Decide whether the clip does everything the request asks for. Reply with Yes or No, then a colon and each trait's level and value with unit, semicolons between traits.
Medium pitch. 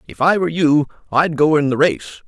Yes: medium, 150 Hz